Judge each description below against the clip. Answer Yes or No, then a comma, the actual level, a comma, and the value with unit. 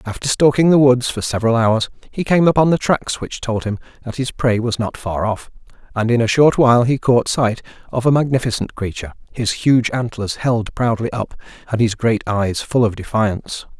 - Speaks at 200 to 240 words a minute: Yes, fast, 205 wpm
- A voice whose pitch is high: No, low, 120 Hz